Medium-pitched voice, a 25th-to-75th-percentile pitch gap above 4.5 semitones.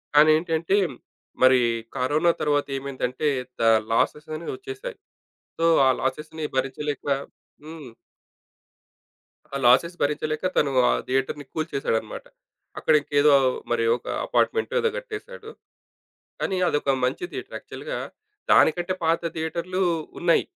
No: medium, 155 Hz; average, 3.8 semitones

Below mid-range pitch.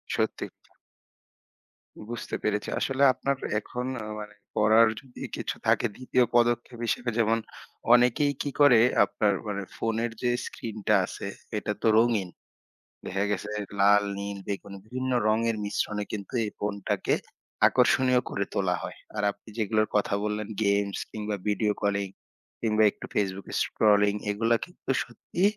Yes: low, 110 Hz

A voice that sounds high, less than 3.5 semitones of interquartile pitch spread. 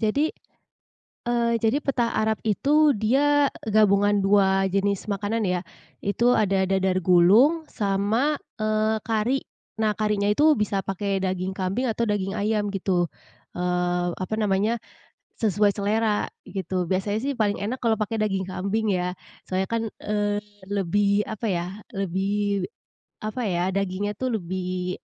Yes: high, 205 Hz; narrow, 2.4 semitones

